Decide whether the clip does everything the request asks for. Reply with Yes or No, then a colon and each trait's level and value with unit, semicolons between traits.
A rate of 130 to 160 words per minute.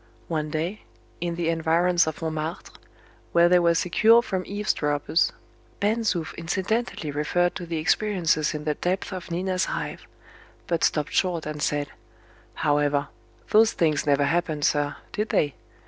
Yes: average, 145 wpm